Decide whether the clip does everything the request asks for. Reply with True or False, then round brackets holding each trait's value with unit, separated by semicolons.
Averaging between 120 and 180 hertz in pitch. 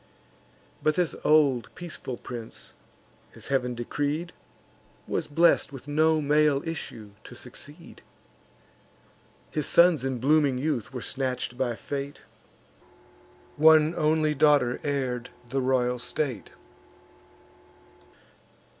True (140 Hz)